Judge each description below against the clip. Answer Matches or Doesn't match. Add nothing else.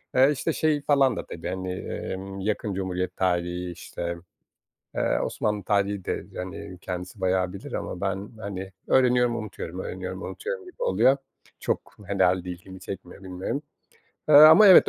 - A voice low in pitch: Matches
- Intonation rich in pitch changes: Matches